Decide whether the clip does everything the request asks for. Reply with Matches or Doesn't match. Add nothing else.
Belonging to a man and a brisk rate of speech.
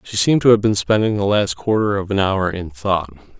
Matches